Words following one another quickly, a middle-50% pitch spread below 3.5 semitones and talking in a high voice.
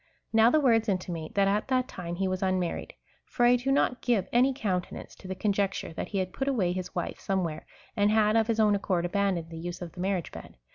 No: fast, 245 wpm; average, 3.8 semitones; high, 195 Hz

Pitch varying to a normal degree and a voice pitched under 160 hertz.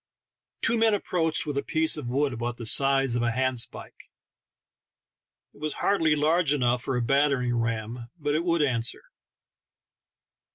Yes: average, 4.3 semitones; low, 135 Hz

